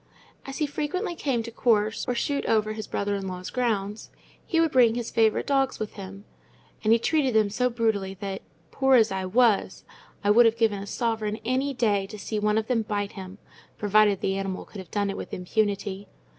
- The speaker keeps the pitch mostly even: No, average, 3.2 semitones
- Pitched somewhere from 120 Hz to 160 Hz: No, high, 215 Hz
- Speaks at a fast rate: Yes, fast, 210 wpm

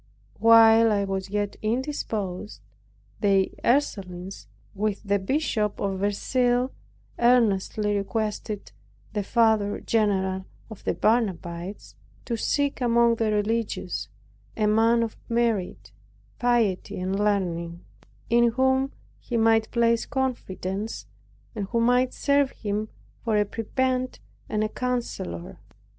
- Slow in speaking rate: Yes, slow, 115 wpm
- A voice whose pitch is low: No, high, 215 Hz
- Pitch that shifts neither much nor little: Yes, average, 3.2 semitones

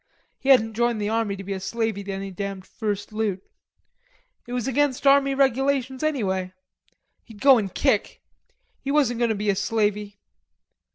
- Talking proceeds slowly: No, average, 170 wpm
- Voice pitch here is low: No, high, 220 Hz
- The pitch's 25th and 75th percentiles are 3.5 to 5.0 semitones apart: Yes, average, 4.6 semitones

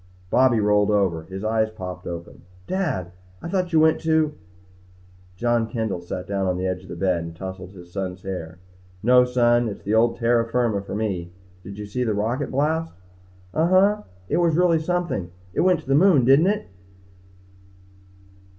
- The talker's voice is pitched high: No, low, 110 Hz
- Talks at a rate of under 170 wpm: No, average, 185 wpm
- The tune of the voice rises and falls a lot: Yes, wide, 7.9 semitones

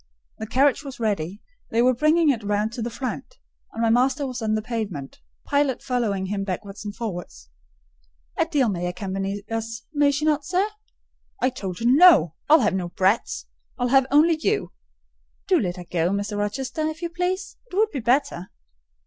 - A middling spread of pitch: No, wide, 6.1 semitones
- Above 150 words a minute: Yes, average, 180 wpm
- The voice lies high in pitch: Yes, high, 230 Hz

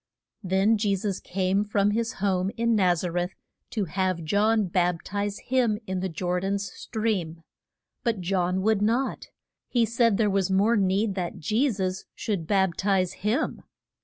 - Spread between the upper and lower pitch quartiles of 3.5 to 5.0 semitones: No, average, 2.8 semitones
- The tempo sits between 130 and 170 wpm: Yes, average, 165 wpm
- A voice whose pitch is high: Yes, high, 195 Hz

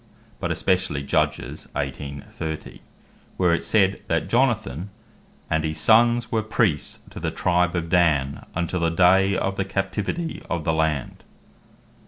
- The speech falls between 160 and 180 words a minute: No, average, 150 wpm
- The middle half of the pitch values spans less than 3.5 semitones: No, average, 3.9 semitones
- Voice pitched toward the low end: Yes, very low, 90 Hz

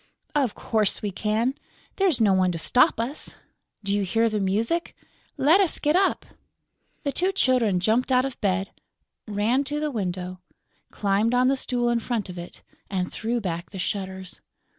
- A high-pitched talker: Yes, high, 225 Hz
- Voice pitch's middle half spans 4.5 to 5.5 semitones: Yes, average, 5.1 semitones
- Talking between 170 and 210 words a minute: Yes, average, 175 wpm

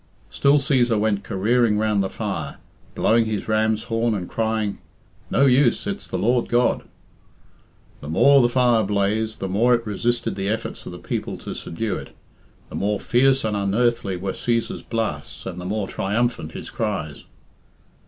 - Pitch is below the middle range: Yes, low, 110 Hz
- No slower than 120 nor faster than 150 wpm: No, average, 165 wpm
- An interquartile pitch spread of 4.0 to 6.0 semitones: No, average, 3.2 semitones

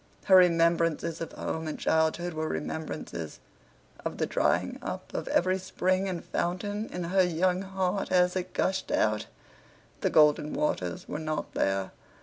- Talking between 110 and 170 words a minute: Yes, average, 150 wpm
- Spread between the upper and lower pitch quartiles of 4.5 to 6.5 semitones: No, average, 2.9 semitones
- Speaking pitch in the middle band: Yes, medium, 170 Hz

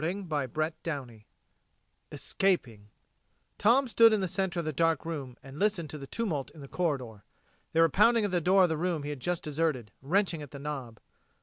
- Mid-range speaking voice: Yes, medium, 160 Hz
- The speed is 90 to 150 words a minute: No, average, 195 wpm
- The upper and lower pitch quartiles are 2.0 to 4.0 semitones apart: No, average, 5.1 semitones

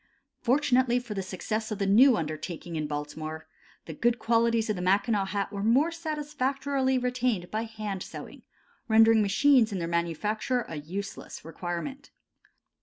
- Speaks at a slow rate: No, average, 150 wpm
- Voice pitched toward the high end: Yes, high, 215 Hz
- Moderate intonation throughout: No, wide, 5.7 semitones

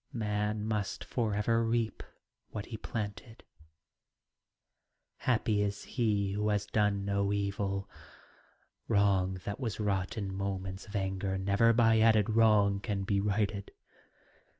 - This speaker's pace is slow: Yes, slow, 125 wpm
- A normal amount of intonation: No, narrow, 1.8 semitones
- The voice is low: Yes, low, 105 Hz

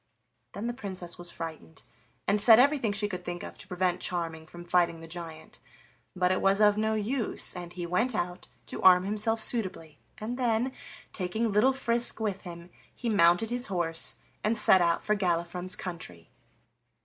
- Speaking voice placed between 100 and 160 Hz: No, medium, 185 Hz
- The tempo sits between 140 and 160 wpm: No, average, 175 wpm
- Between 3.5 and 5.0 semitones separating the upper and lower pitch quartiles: Yes, average, 4.0 semitones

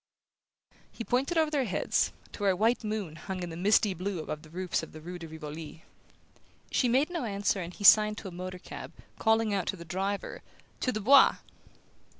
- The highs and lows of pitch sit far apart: No, average, 4.1 semitones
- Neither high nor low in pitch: No, high, 195 Hz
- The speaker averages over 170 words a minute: Yes, fast, 205 wpm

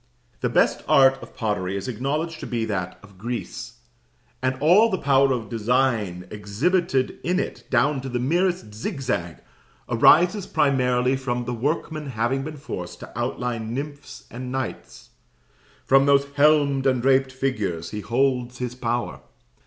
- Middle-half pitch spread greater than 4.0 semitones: No, average, 3.4 semitones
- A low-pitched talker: Yes, low, 130 Hz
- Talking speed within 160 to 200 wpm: No, average, 150 wpm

